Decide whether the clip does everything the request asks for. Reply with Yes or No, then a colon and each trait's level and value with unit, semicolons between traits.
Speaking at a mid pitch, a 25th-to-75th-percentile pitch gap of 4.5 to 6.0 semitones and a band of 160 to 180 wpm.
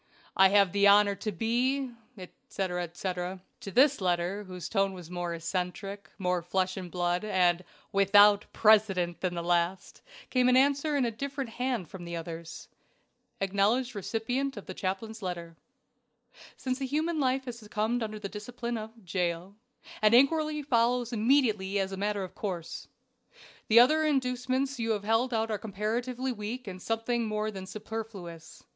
No: high, 210 Hz; average, 4.8 semitones; average, 165 wpm